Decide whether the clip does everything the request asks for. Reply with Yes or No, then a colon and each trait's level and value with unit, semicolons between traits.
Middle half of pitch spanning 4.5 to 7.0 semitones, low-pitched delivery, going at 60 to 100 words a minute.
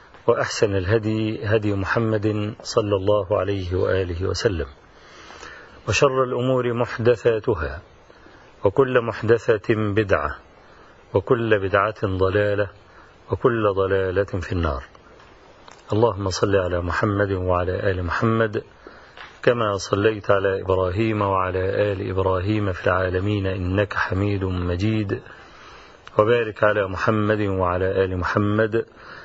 No: narrow, 2.5 semitones; low, 105 Hz; average, 95 wpm